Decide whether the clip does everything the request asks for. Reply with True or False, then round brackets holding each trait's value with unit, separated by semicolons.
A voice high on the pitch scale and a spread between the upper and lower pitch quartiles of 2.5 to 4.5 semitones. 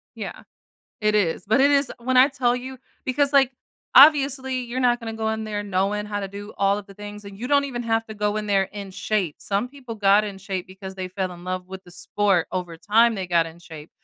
True (210 Hz; 4.2 semitones)